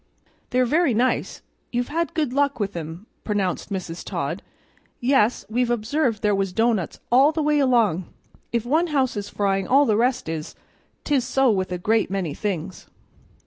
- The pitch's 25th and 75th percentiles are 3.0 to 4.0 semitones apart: No, average, 5.3 semitones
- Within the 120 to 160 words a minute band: No, average, 170 wpm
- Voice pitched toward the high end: Yes, high, 230 Hz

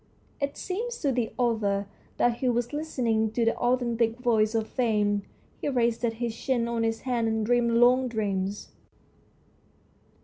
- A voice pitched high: Yes, high, 235 Hz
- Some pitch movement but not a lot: No, narrow, 2.0 semitones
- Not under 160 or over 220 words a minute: No, average, 150 wpm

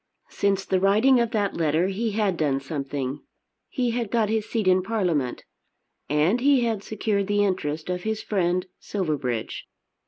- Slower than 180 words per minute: Yes, average, 160 wpm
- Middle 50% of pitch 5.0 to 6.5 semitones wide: Yes, wide, 5.6 semitones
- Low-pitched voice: No, high, 195 Hz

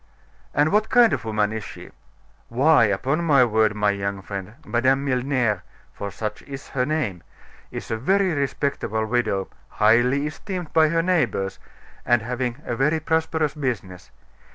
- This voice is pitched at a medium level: No, low, 125 Hz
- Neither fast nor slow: Yes, average, 155 wpm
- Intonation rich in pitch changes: Yes, wide, 6.1 semitones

